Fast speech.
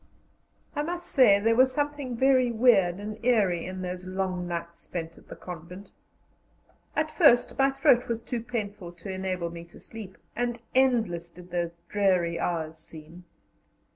No: average, 160 wpm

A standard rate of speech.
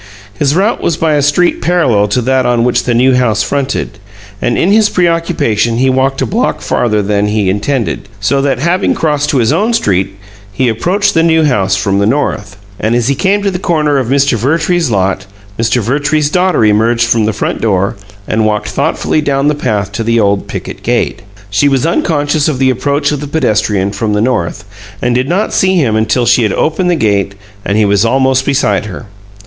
No: fast, 210 wpm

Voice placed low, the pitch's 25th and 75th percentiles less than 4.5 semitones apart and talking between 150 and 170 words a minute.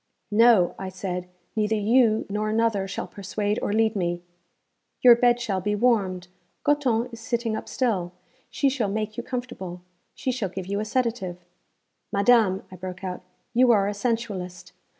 No: high, 210 Hz; average, 3.9 semitones; average, 165 wpm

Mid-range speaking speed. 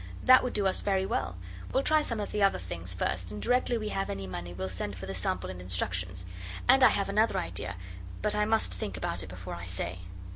No: fast, 240 wpm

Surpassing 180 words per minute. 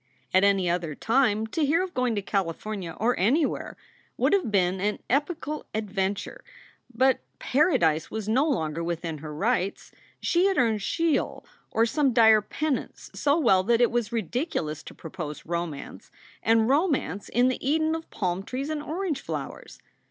No: average, 165 wpm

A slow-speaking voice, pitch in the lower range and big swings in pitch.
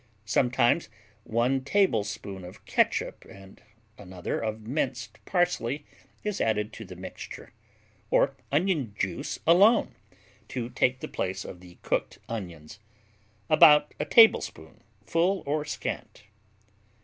Yes: slow, 115 wpm; low, 115 Hz; wide, 7.2 semitones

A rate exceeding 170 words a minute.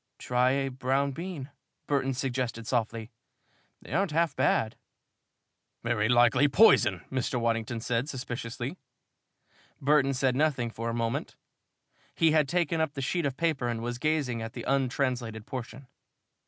No: average, 140 wpm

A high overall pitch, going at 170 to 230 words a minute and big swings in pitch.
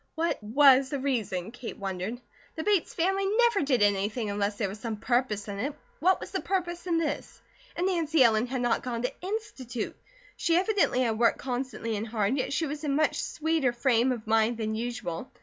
Yes: very high, 250 Hz; average, 200 wpm; wide, 6.4 semitones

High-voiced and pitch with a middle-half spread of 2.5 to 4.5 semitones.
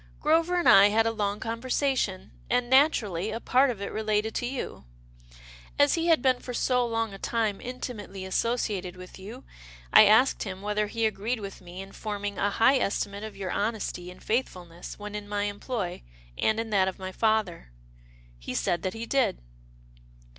Yes: high, 215 Hz; average, 3.7 semitones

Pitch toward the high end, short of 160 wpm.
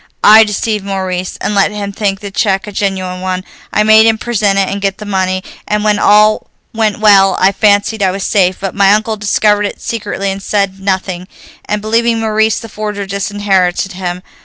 No: high, 200 Hz; average, 190 wpm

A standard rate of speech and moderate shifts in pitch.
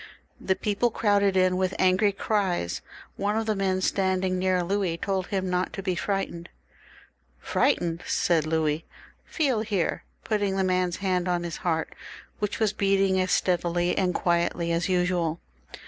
No: average, 165 wpm; narrow, 2.1 semitones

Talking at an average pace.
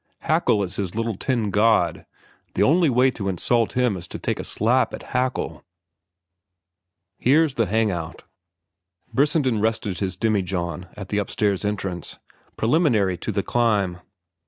Yes: average, 145 wpm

